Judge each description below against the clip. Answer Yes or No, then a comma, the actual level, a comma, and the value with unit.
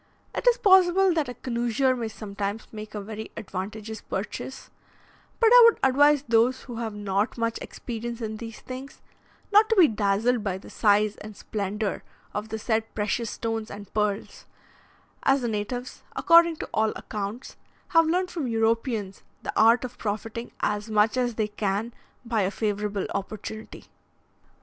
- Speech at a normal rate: Yes, average, 160 wpm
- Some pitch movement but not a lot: Yes, average, 3.4 semitones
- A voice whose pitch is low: No, high, 225 Hz